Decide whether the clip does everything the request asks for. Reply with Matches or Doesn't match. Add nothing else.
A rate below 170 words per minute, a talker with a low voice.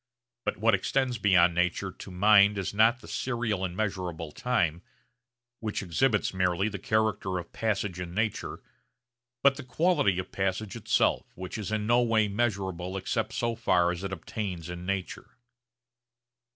Matches